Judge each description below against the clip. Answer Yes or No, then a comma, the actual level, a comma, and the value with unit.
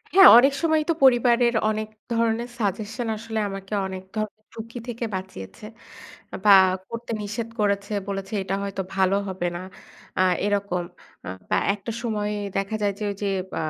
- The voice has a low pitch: No, high, 210 Hz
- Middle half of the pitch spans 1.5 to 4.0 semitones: Yes, average, 2.9 semitones